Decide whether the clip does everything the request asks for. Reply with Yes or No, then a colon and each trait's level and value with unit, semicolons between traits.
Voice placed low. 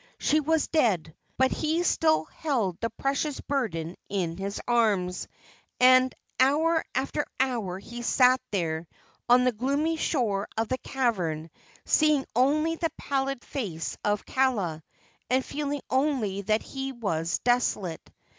No: very high, 250 Hz